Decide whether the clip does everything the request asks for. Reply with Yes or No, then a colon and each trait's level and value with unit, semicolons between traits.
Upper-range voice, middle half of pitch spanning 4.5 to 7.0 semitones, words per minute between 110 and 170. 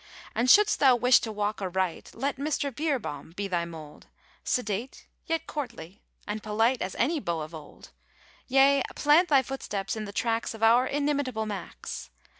Yes: high, 230 Hz; wide, 5.6 semitones; average, 165 wpm